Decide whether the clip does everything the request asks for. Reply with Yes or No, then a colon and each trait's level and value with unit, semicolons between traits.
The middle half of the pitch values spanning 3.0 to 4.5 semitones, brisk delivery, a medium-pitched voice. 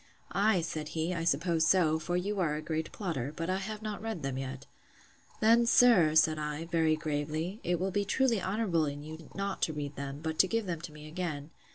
Yes: average, 4.0 semitones; fast, 220 wpm; medium, 165 Hz